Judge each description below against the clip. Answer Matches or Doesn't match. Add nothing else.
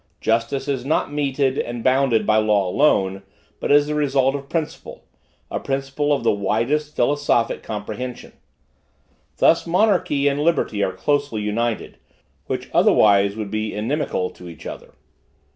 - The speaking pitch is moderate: Doesn't match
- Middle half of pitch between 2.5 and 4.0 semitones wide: Doesn't match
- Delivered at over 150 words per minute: Doesn't match